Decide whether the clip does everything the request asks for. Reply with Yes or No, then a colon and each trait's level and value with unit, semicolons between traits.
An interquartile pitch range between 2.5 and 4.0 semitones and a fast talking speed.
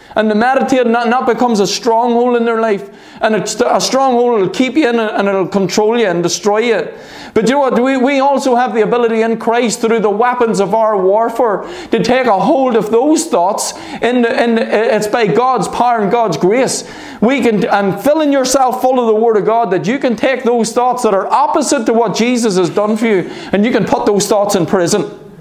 Yes: average, 2.9 semitones; fast, 215 wpm